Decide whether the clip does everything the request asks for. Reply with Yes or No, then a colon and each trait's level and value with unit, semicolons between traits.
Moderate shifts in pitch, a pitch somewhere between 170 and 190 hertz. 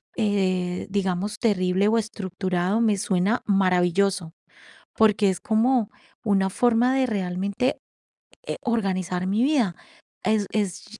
No: average, 3.0 semitones; high, 200 Hz